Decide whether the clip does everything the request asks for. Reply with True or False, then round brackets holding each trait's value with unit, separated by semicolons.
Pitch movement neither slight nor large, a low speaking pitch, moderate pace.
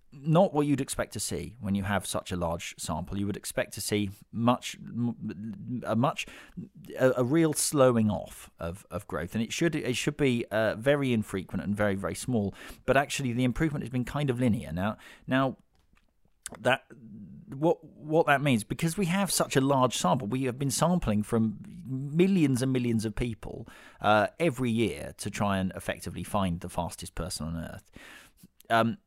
False (5.7 semitones; 120 Hz; 185 wpm)